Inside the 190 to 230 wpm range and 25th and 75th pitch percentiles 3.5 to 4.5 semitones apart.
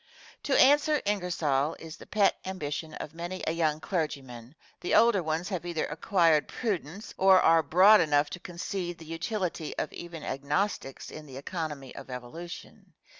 No: average, 160 wpm; average, 3.8 semitones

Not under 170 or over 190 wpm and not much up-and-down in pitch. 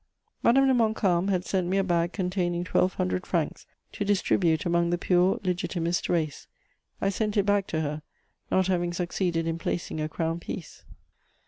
Yes: average, 175 wpm; narrow, 2.3 semitones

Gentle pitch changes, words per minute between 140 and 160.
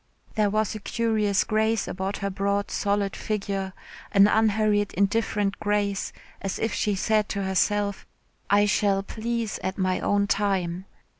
Yes: narrow, 1.5 semitones; average, 145 wpm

